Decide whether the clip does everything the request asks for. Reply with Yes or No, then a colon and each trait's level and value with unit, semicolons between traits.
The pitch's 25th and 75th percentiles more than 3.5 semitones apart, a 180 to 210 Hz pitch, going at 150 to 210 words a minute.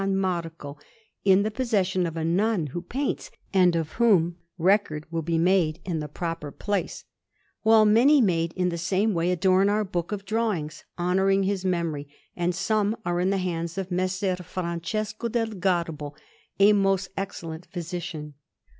No: average, 3.1 semitones; medium, 185 Hz; average, 160 wpm